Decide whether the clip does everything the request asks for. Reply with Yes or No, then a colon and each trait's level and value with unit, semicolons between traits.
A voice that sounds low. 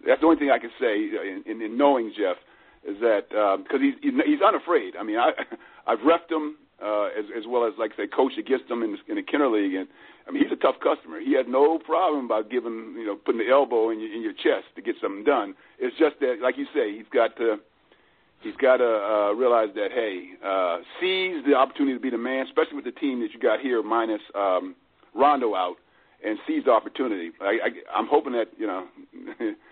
No: very high, 315 Hz